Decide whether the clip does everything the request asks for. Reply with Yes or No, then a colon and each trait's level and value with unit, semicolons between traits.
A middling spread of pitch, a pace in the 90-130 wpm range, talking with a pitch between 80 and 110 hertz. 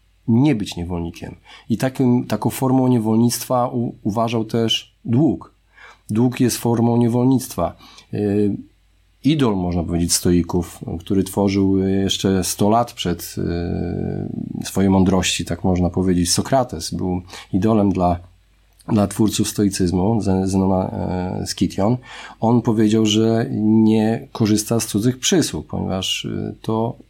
Yes: average, 4.0 semitones; average, 115 wpm; low, 105 Hz